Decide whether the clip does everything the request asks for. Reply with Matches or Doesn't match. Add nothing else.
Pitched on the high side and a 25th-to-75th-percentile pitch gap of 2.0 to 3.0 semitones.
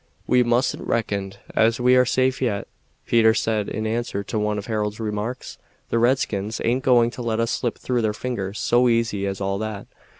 Doesn't match